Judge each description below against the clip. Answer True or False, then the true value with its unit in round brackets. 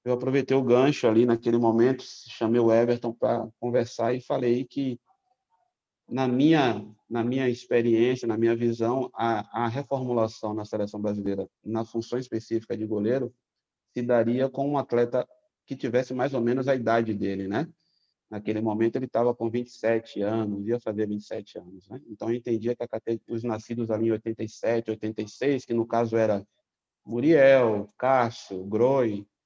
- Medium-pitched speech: False (115 Hz)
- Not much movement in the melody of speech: True (2.2 semitones)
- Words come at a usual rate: True (160 wpm)